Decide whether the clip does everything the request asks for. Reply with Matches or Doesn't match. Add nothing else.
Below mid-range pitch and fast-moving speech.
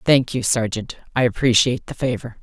Doesn't match